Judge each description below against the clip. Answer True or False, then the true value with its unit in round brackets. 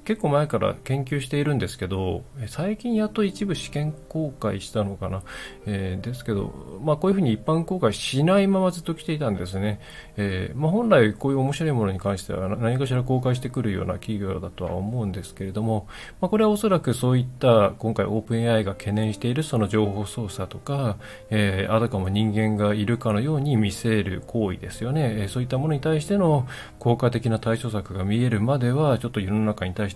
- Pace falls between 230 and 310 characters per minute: False (435 characters per minute)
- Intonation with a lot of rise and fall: True (5.7 semitones)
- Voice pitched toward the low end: True (115 Hz)